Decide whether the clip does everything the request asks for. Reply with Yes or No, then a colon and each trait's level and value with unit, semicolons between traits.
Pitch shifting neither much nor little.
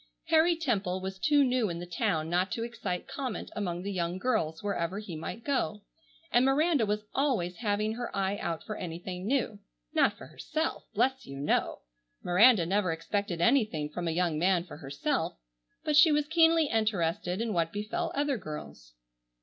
No: wide, 6.6 semitones